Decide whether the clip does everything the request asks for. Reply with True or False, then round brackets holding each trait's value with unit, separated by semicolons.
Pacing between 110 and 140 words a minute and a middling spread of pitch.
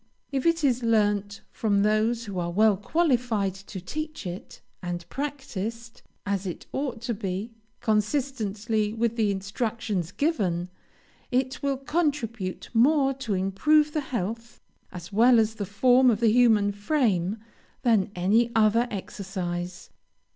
True (135 wpm; 4.1 semitones)